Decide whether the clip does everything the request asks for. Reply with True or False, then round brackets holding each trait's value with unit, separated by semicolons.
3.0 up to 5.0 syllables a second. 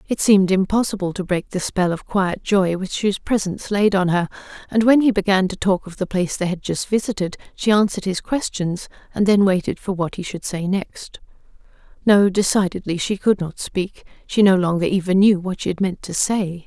False (5.3 syllables/s)